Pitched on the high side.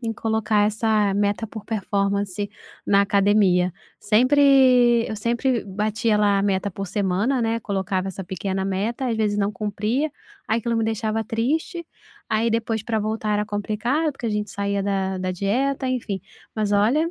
Yes: high, 210 Hz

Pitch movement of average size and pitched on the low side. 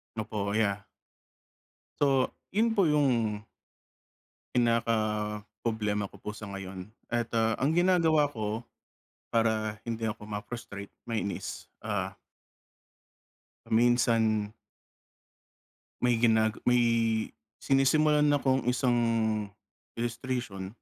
Yes: average, 3.4 semitones; low, 115 Hz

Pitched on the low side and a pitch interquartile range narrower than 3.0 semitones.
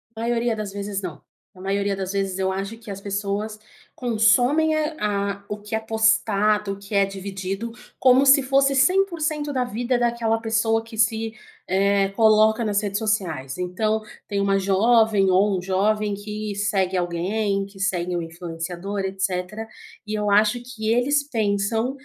No: high, 210 Hz; narrow, 2.4 semitones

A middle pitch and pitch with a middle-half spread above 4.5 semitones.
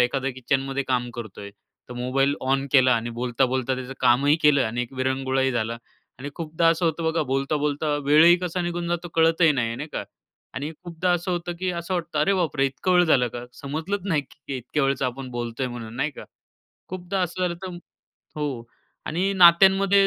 Yes: medium, 145 Hz; average, 4.9 semitones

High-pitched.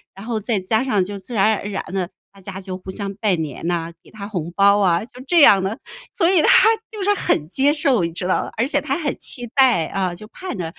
Yes: high, 200 Hz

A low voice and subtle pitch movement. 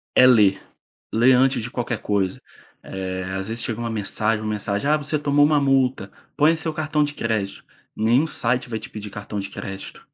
No: low, 115 Hz; average, 5.2 semitones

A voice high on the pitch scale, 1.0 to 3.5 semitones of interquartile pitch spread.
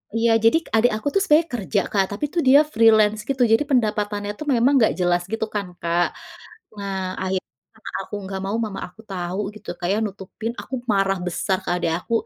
Yes: high, 210 Hz; average, 2.9 semitones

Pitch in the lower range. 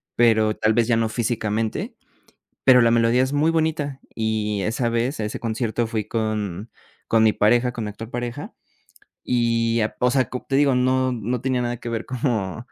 Yes: low, 115 Hz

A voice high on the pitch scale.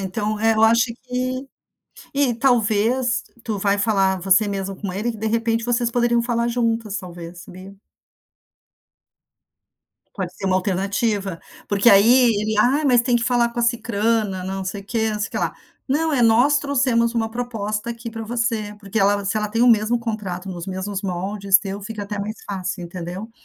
Yes: high, 220 Hz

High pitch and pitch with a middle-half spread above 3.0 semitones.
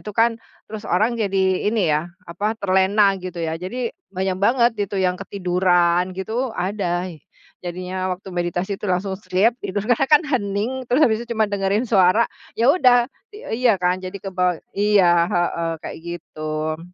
Yes: high, 195 Hz; average, 3.4 semitones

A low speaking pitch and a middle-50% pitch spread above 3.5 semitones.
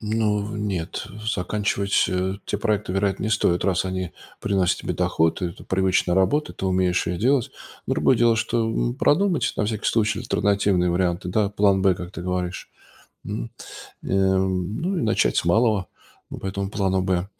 No: very low, 95 Hz; average, 2.7 semitones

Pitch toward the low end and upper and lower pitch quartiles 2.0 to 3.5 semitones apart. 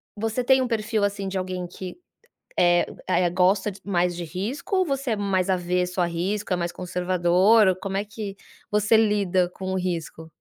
No: high, 190 Hz; average, 2.8 semitones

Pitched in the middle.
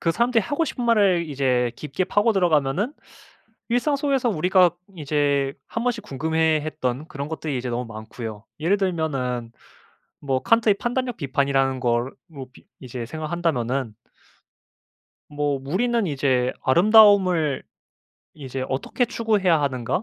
Yes: medium, 155 Hz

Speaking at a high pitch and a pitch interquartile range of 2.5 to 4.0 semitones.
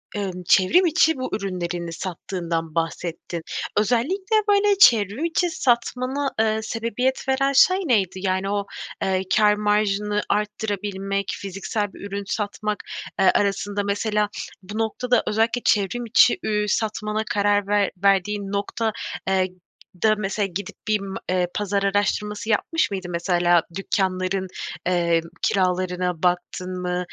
Yes: high, 205 Hz; average, 2.9 semitones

